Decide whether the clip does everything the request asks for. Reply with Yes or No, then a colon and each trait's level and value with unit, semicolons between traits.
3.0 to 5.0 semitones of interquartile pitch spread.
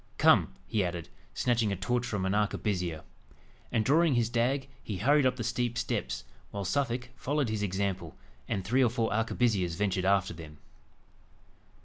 Yes: average, 4.5 semitones